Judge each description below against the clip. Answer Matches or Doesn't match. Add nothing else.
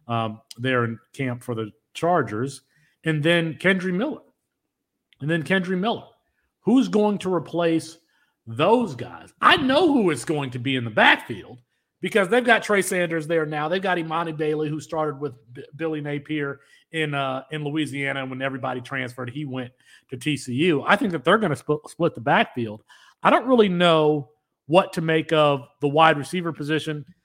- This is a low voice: Doesn't match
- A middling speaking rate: Matches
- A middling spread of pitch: Matches